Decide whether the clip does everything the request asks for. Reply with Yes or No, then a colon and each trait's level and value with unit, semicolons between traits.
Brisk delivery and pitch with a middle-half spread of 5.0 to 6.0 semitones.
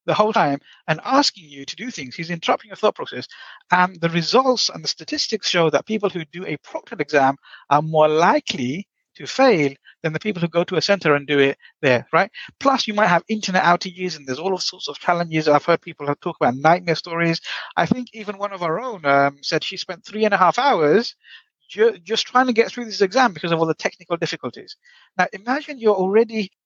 Yes: fast, 225 wpm; average, 5.3 semitones